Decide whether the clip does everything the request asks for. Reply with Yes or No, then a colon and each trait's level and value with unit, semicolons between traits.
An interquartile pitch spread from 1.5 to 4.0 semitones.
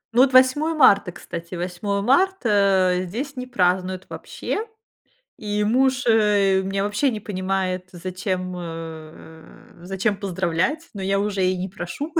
Yes: average, 3.6 semitones